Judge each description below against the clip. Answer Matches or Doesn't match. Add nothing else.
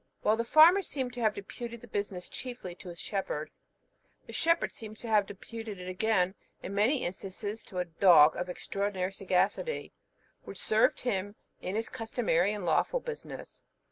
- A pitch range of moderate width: Matches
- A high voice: Matches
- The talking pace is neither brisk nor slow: Matches